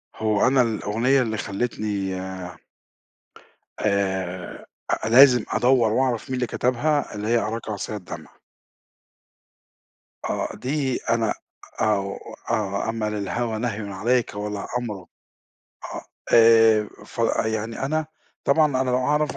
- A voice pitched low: Yes, low, 115 Hz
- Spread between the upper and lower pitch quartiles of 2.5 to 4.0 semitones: Yes, average, 3.3 semitones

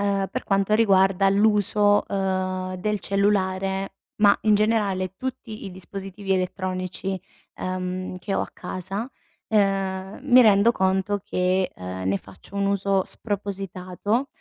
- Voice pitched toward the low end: No, high, 195 Hz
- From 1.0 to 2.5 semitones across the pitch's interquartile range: Yes, narrow, 1.7 semitones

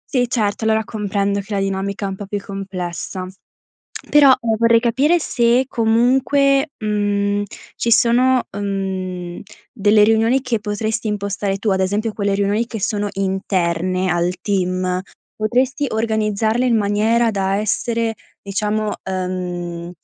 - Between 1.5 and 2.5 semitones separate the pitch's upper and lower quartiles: No, average, 2.9 semitones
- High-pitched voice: Yes, high, 210 Hz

